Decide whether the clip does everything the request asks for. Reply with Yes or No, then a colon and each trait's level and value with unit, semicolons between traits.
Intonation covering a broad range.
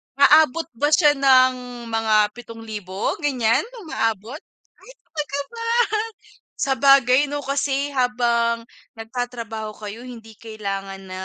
No: average, 3.9 semitones